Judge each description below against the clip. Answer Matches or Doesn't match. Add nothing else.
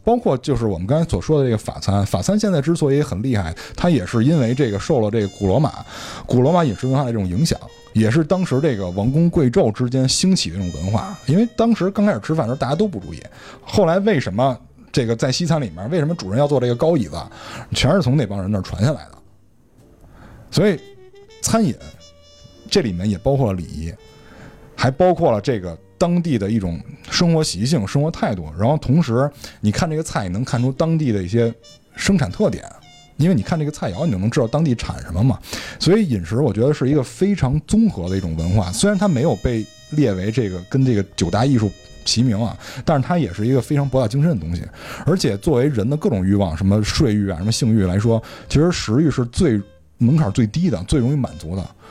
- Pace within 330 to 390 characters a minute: Matches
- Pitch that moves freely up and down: Matches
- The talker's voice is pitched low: Matches